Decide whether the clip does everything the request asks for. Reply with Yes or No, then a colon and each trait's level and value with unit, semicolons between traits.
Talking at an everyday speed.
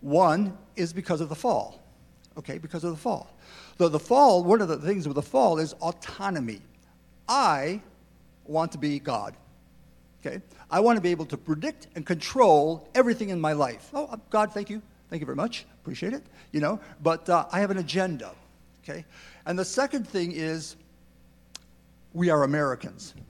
Yes: average, 180 wpm